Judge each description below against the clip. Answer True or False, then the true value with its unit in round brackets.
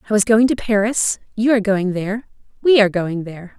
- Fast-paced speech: False (185 wpm)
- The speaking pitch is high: True (210 Hz)